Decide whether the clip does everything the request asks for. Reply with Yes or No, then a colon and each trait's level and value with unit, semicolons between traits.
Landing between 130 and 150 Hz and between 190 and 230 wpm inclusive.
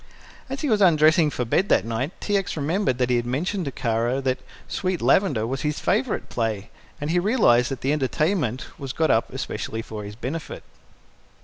Yes: medium, 140 Hz; average, 195 wpm